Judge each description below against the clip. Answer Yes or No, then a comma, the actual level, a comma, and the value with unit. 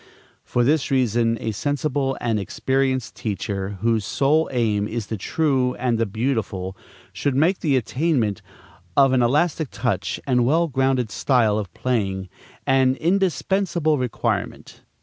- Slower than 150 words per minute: Yes, slow, 135 wpm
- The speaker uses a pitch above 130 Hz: No, low, 125 Hz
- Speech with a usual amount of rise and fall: Yes, average, 4.3 semitones